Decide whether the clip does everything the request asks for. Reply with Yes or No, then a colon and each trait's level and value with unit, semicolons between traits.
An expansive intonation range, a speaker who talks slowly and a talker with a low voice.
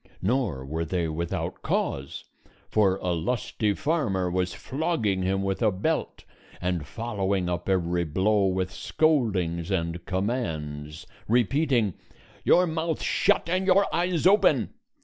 Yes: wide, 6.3 semitones; slow, 130 wpm; very low, 95 Hz